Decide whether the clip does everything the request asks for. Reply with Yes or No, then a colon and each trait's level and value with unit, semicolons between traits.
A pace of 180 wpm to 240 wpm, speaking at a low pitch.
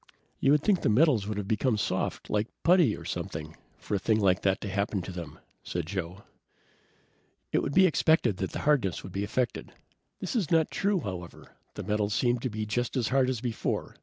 Yes: average, 200 wpm; low, 110 Hz